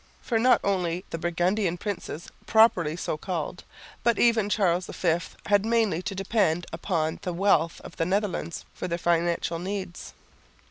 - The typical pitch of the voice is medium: Yes, medium, 180 Hz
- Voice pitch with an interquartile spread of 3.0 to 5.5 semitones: Yes, average, 3.3 semitones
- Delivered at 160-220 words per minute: No, average, 150 wpm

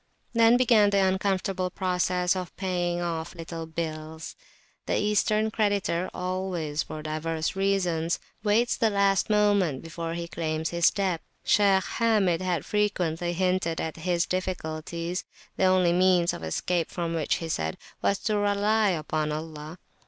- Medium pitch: Yes, medium, 180 Hz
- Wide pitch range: No, average, 3.2 semitones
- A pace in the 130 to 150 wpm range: Yes, average, 145 wpm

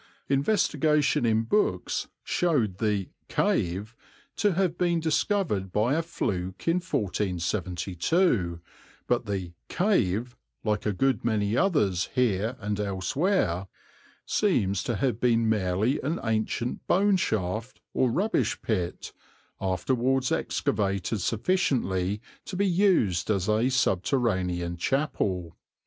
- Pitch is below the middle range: Yes, low, 110 Hz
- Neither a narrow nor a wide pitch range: No, wide, 7.4 semitones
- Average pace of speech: No, slow, 110 wpm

